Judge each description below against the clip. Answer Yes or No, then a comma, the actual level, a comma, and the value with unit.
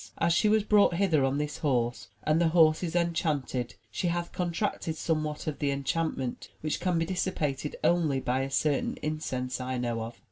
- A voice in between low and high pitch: Yes, medium, 155 Hz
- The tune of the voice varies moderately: Yes, average, 4.2 semitones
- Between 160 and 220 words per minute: Yes, average, 185 wpm